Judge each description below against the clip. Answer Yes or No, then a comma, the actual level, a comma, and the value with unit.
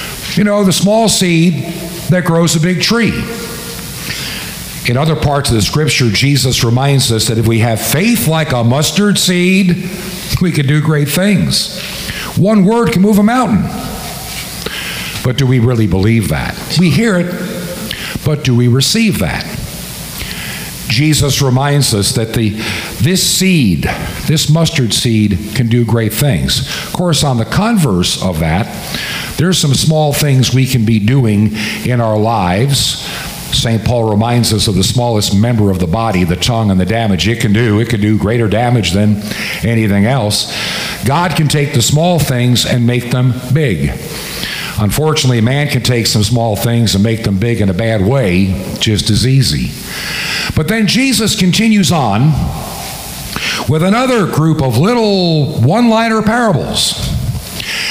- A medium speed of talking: Yes, average, 155 wpm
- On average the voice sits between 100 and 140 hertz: Yes, low, 135 Hz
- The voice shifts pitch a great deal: Yes, wide, 7.3 semitones